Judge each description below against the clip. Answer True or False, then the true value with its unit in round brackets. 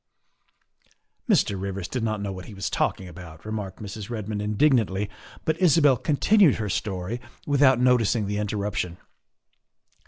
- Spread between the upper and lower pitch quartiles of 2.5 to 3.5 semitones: False (4.4 semitones)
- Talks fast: False (155 wpm)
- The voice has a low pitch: True (105 Hz)